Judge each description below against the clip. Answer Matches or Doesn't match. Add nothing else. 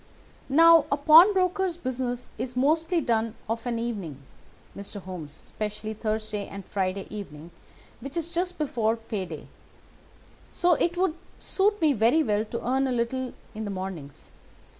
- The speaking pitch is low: Doesn't match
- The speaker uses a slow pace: Doesn't match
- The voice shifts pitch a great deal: Matches